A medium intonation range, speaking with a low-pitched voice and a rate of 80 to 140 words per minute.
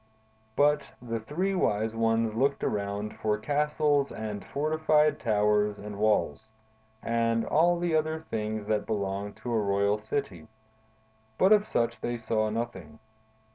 No: wide, 5.7 semitones; low, 115 Hz; slow, 135 wpm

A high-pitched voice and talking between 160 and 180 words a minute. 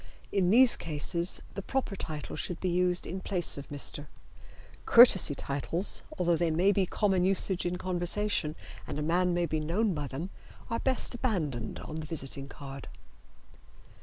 No: medium, 175 Hz; average, 165 wpm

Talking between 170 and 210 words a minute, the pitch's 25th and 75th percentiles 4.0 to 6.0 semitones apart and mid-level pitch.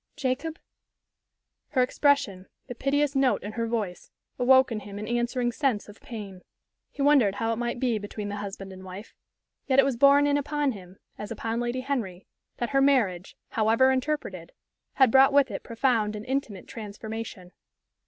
No: average, 175 wpm; average, 4.7 semitones; high, 235 Hz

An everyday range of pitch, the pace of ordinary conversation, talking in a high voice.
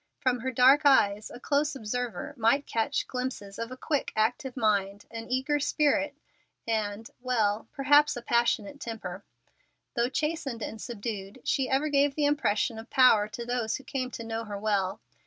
Yes: average, 4.0 semitones; average, 170 wpm; high, 240 Hz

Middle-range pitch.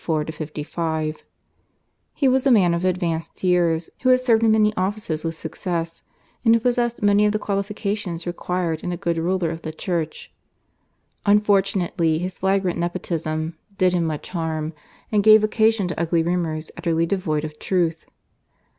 Yes: medium, 180 Hz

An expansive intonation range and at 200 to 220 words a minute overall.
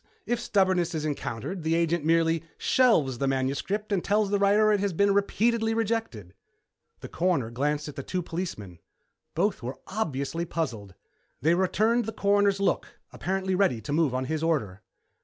No: wide, 6.3 semitones; average, 165 wpm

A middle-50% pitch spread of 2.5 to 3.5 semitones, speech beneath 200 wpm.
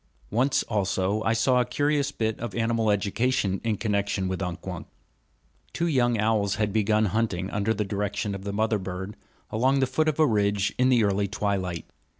Yes: average, 2.9 semitones; average, 180 wpm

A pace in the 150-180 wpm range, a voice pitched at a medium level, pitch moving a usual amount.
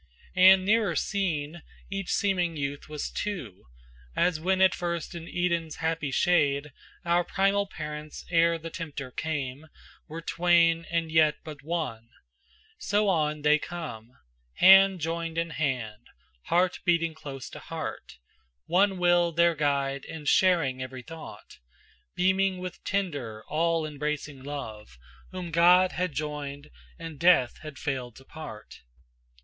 No: slow, 135 wpm; medium, 165 Hz; average, 3.4 semitones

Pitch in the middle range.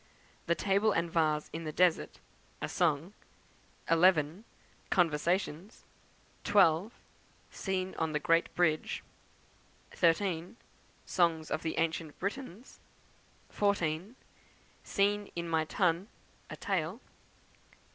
Yes: medium, 170 Hz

